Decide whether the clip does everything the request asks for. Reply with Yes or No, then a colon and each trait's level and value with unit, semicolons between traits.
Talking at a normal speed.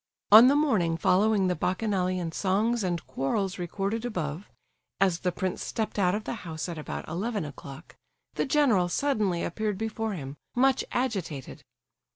Yes: average, 155 wpm